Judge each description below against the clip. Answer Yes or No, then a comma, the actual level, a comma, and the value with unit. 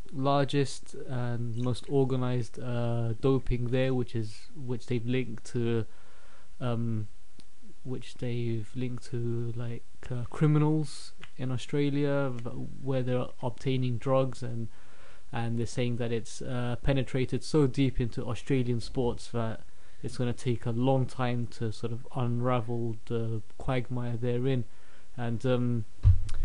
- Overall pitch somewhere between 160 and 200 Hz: No, low, 120 Hz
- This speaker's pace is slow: Yes, slow, 130 wpm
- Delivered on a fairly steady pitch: Yes, narrow, 2.0 semitones